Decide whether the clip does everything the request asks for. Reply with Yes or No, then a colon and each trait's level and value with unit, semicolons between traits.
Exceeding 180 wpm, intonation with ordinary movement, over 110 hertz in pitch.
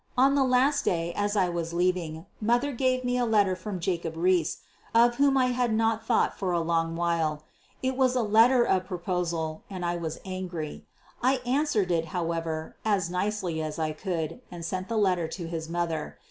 No: average, 190 wpm; wide, 5.7 semitones; medium, 185 Hz